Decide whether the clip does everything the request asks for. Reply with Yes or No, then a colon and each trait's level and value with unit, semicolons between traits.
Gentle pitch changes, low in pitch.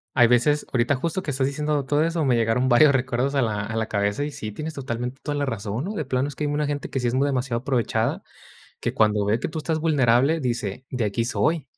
No: average, 3.8 semitones; low, 130 Hz